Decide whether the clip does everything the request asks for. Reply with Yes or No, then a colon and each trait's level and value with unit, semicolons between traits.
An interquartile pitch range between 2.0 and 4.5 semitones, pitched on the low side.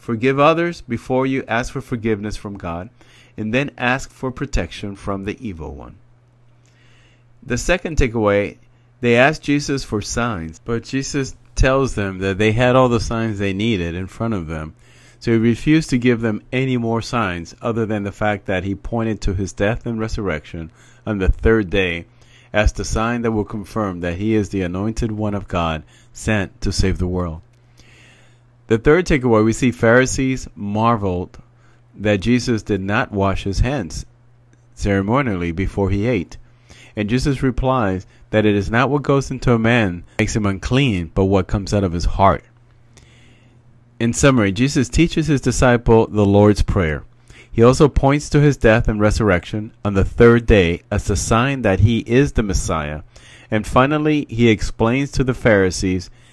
Yes: average, 3.4 semitones; low, 115 Hz